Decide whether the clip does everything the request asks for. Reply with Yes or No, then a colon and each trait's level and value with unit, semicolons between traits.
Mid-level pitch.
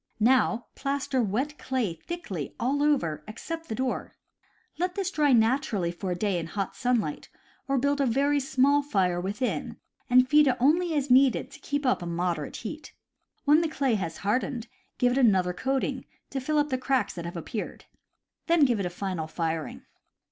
No: very high, 255 Hz